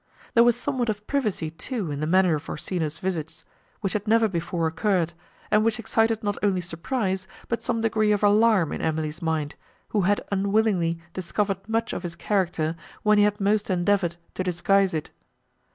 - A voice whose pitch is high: Yes, high, 195 Hz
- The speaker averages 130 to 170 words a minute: No, average, 180 wpm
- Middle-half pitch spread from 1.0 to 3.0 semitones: No, average, 4.2 semitones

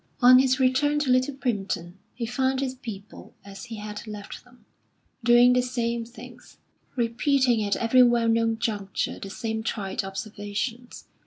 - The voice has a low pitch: No, high, 235 Hz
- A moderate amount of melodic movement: Yes, average, 3.2 semitones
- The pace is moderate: Yes, average, 155 wpm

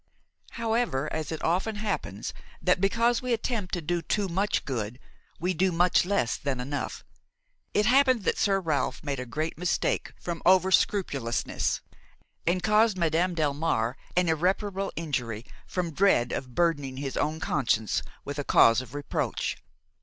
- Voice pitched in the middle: Yes, medium, 170 Hz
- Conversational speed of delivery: Yes, average, 155 wpm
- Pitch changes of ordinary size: No, wide, 5.8 semitones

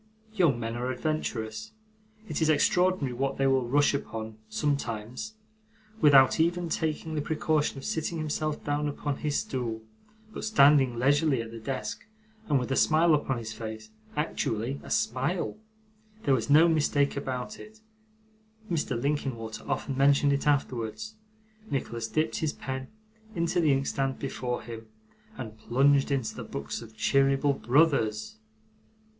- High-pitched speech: No, low, 135 Hz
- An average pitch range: Yes, average, 4.4 semitones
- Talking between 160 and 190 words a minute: No, average, 145 wpm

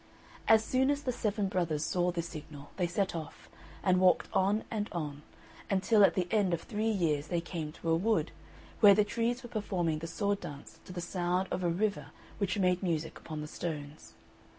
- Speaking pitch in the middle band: Yes, medium, 180 Hz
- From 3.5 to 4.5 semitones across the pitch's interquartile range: Yes, average, 3.9 semitones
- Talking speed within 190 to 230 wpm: Yes, average, 200 wpm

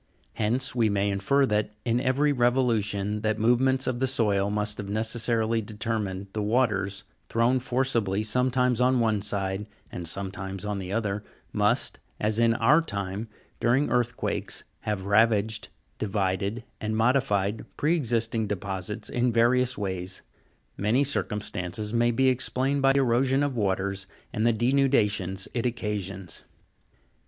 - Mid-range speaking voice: No, low, 110 Hz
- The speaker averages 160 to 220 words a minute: No, average, 140 wpm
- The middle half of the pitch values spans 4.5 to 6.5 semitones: No, average, 3.6 semitones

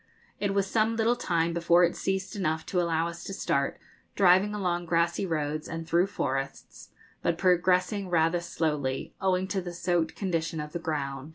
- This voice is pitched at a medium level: Yes, medium, 175 Hz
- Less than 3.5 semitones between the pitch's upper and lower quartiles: Yes, average, 2.8 semitones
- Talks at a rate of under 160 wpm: No, average, 175 wpm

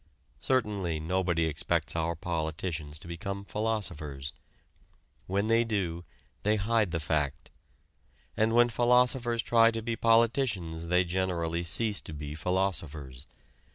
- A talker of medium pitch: No, very low, 90 Hz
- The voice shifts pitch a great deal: Yes, wide, 5.7 semitones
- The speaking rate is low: Yes, slow, 120 wpm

